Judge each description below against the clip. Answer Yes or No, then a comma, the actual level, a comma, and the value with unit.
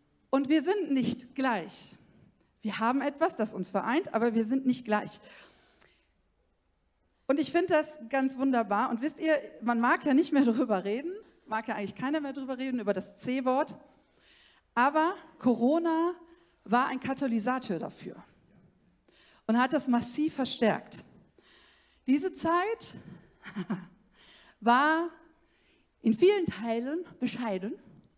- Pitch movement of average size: No, wide, 5.9 semitones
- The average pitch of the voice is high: Yes, very high, 260 Hz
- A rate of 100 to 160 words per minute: Yes, average, 130 wpm